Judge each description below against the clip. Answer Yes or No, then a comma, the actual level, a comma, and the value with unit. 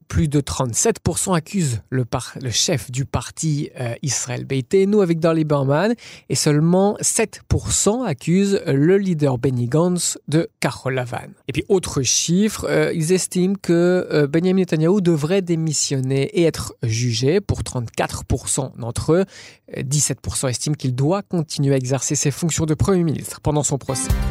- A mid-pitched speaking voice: Yes, medium, 150 Hz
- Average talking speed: Yes, average, 155 wpm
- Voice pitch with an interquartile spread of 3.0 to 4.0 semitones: No, average, 4.9 semitones